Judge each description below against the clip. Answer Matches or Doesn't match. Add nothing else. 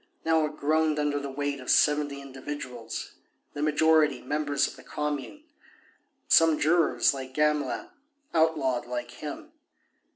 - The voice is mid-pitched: Matches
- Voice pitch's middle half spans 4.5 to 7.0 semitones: Doesn't match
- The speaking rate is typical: Doesn't match